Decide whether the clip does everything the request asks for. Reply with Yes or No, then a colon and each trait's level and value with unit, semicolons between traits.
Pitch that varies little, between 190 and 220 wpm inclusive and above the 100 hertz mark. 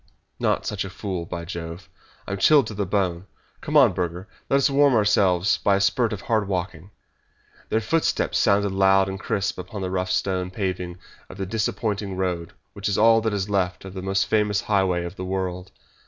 No: narrow, 2.3 semitones; average, 200 wpm; very low, 95 Hz